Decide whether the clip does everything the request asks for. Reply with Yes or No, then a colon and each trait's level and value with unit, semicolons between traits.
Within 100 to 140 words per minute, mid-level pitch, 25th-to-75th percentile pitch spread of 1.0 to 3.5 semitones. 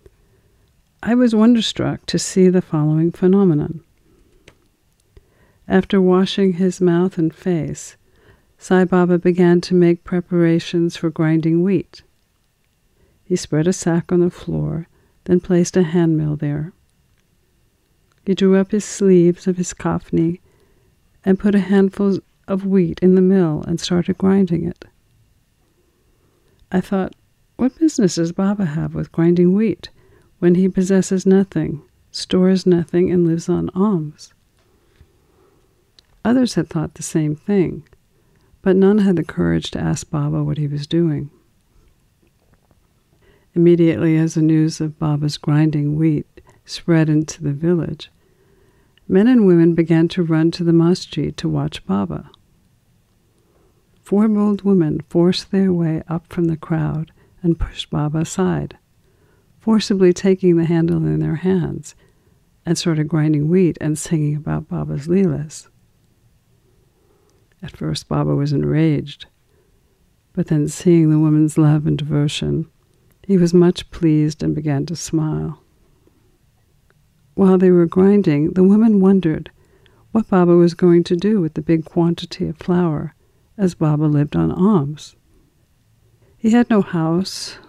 Yes: slow, 135 wpm; medium, 170 Hz; average, 3.2 semitones